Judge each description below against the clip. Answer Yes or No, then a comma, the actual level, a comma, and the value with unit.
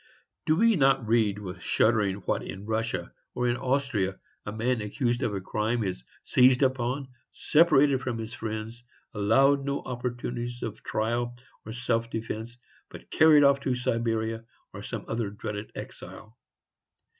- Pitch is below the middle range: Yes, low, 120 Hz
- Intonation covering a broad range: No, average, 3.0 semitones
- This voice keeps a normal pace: Yes, average, 150 wpm